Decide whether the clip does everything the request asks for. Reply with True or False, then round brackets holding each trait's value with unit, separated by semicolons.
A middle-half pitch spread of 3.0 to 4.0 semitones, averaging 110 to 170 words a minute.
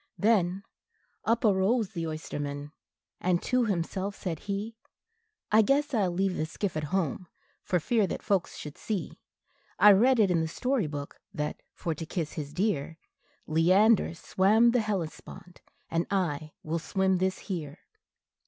False (4.4 semitones; 155 wpm)